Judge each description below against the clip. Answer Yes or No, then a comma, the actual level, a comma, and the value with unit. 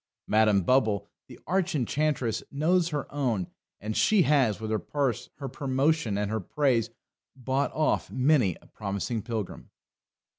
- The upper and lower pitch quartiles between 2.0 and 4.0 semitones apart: No, average, 5.2 semitones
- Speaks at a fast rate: No, average, 145 wpm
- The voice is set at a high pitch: No, low, 130 Hz